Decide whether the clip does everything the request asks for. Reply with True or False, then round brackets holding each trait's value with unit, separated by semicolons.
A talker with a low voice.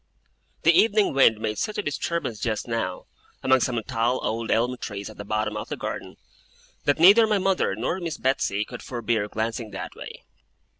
True (120 Hz)